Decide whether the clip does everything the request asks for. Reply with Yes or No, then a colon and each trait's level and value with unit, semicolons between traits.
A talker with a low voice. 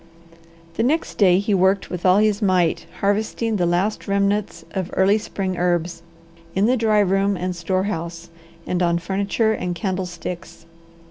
No: high, 190 Hz